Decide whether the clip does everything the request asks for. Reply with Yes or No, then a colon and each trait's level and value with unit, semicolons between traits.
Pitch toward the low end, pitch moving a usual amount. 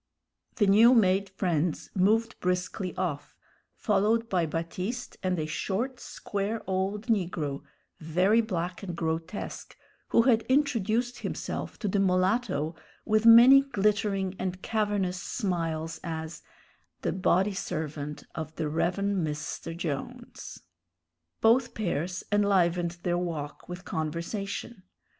No: medium, 185 Hz; average, 4.1 semitones